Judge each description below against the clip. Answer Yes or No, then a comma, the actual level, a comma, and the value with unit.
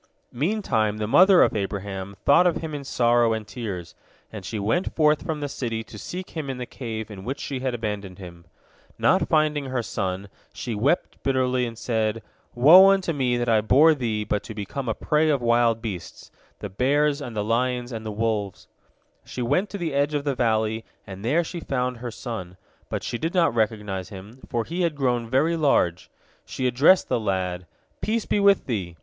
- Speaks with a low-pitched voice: Yes, low, 120 Hz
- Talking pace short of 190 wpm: No, average, 200 wpm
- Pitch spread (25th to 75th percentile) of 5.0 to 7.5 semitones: Yes, average, 5.3 semitones